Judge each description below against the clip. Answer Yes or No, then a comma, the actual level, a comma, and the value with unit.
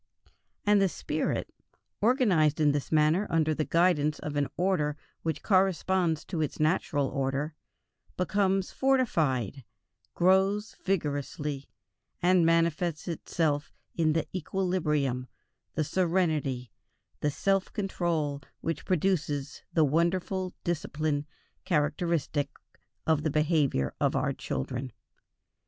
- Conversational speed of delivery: No, slow, 110 wpm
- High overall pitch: No, medium, 160 Hz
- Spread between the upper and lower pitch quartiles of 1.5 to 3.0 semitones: No, average, 4.0 semitones